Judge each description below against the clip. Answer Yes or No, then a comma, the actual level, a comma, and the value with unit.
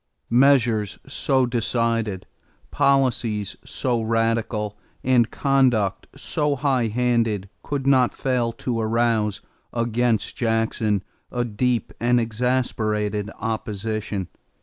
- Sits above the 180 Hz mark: No, low, 115 Hz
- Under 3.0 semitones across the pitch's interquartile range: Yes, narrow, 2.5 semitones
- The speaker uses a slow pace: Yes, slow, 100 wpm